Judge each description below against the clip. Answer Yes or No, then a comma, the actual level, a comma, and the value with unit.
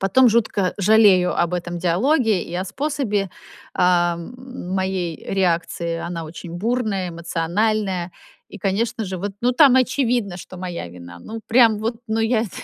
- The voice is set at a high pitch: Yes, high, 195 Hz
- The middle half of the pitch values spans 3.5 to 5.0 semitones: Yes, average, 4.5 semitones